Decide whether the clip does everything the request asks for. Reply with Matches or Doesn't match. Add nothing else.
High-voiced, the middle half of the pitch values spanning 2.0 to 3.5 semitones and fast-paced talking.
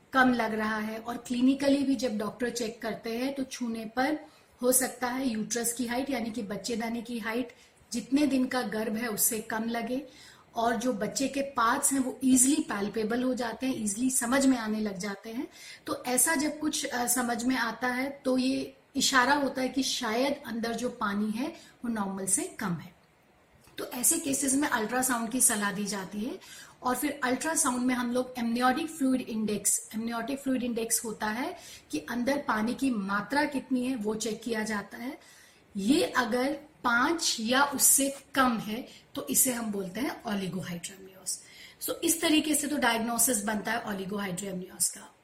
Doesn't match